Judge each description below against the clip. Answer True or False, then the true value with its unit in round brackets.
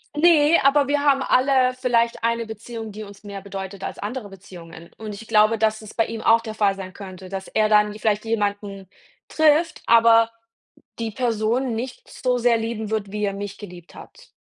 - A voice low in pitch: False (220 Hz)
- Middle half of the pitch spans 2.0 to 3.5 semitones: True (3.0 semitones)